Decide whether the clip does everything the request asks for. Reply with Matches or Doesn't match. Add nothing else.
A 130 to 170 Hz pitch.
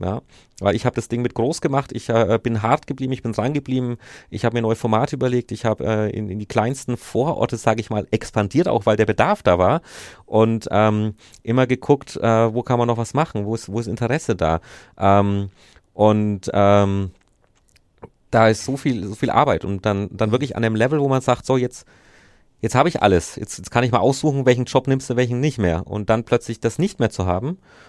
Doesn't match